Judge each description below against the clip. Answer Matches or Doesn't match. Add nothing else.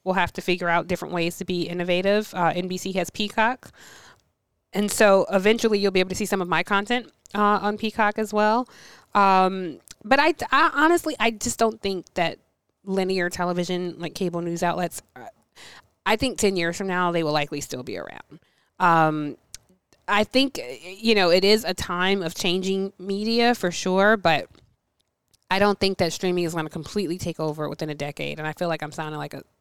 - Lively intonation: Doesn't match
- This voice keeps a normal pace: Matches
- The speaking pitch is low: Doesn't match